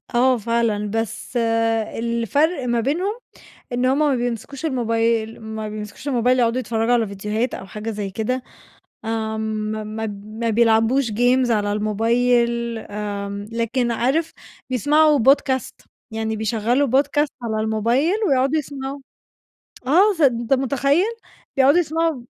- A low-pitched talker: No, high, 235 Hz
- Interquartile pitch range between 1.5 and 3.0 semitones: No, average, 3.4 semitones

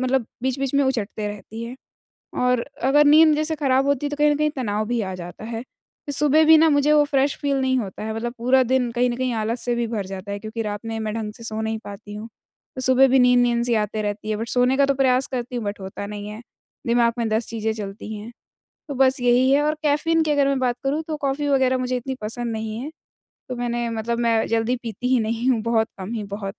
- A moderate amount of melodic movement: Yes, average, 3.4 semitones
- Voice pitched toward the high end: Yes, high, 240 Hz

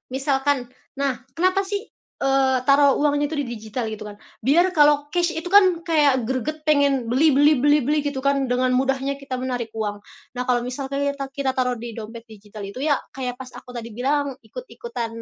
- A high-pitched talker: Yes, very high, 270 Hz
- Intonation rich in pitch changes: No, average, 2.8 semitones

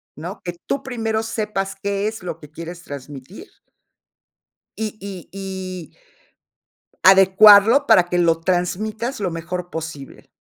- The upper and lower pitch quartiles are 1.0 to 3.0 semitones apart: No, average, 3.8 semitones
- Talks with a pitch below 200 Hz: Yes, high, 190 Hz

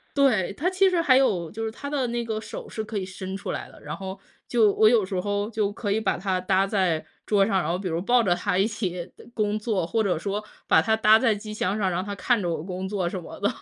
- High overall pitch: Yes, high, 205 Hz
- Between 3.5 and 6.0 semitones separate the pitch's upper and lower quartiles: No, average, 2.9 semitones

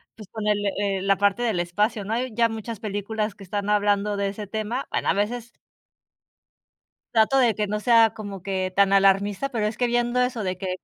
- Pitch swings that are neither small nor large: No, narrow, 2.3 semitones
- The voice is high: Yes, high, 210 Hz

